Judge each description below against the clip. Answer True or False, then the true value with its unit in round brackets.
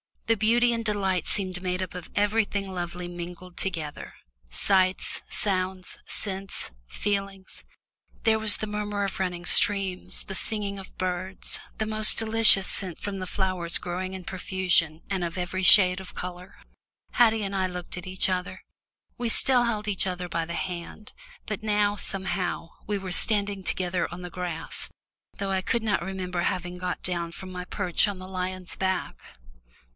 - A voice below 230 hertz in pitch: True (190 Hz)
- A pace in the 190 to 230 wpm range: False (165 wpm)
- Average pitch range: False (2.1 semitones)